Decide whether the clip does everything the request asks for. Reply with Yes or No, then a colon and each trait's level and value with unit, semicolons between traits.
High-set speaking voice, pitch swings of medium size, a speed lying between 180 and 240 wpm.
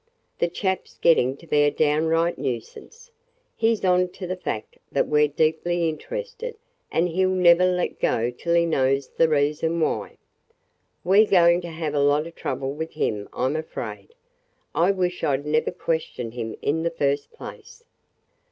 No: medium, 165 Hz; average, 3.7 semitones; average, 185 wpm